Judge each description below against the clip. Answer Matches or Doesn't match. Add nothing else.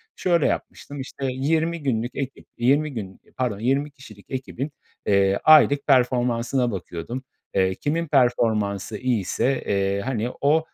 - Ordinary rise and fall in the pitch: Matches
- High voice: Doesn't match